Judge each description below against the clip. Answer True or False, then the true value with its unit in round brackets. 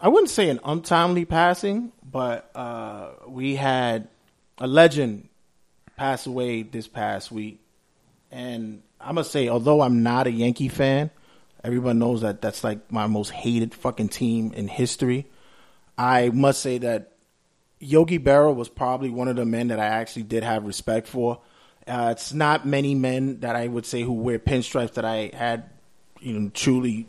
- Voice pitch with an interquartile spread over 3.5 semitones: False (3.1 semitones)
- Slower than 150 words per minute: False (170 wpm)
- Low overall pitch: True (125 Hz)